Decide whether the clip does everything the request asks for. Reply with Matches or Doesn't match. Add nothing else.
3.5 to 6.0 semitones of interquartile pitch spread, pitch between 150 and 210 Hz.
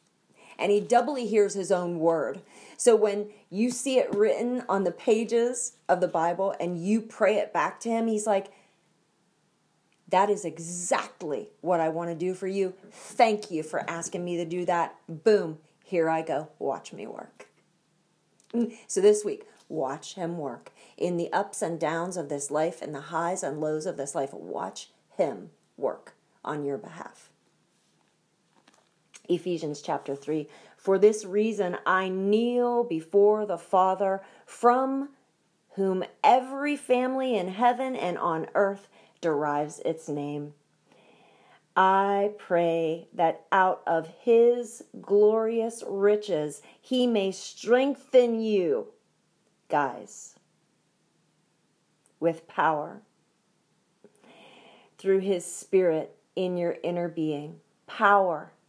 Matches